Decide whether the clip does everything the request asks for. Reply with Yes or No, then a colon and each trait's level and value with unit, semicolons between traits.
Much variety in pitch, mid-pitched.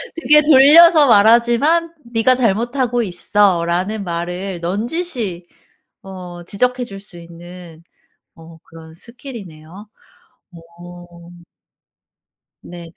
No: wide, 5.9 semitones; high, 195 Hz